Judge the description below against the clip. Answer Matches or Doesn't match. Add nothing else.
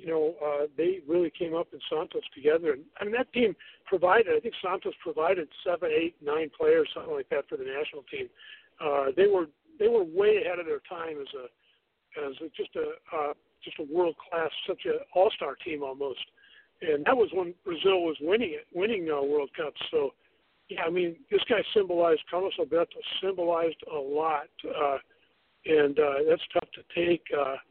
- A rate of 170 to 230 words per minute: Matches